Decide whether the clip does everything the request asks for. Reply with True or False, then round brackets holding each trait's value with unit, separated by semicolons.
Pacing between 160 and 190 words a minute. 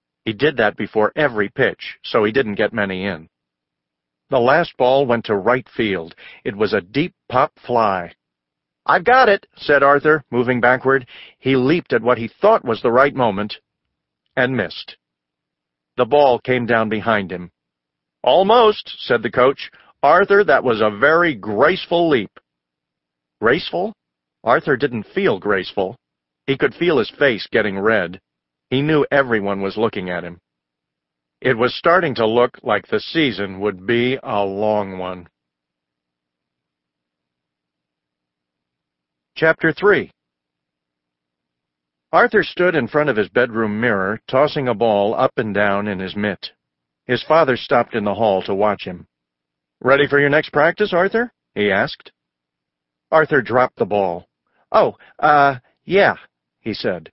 False (145 wpm)